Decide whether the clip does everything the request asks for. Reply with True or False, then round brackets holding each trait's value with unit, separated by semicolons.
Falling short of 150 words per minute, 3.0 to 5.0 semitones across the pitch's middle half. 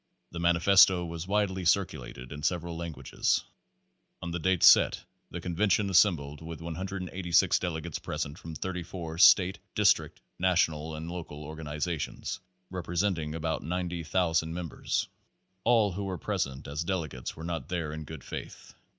False (140 wpm; 2.4 semitones)